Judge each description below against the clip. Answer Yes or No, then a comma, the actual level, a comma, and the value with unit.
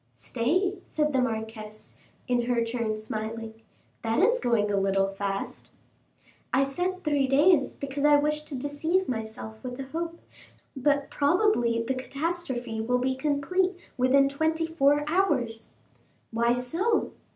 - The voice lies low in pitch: No, very high, 265 Hz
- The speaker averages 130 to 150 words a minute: Yes, average, 140 wpm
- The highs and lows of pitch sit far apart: No, average, 5.0 semitones